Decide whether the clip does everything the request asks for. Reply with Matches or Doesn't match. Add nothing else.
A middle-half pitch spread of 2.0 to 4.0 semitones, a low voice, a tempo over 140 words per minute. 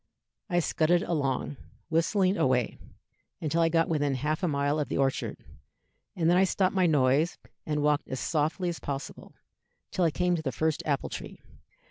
Doesn't match